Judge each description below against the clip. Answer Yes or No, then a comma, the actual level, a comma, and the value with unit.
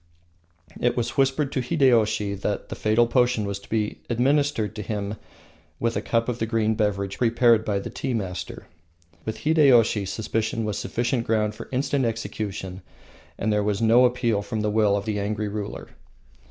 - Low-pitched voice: Yes, low, 110 Hz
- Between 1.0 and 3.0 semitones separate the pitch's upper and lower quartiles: Yes, average, 2.7 semitones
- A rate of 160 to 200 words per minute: Yes, average, 175 wpm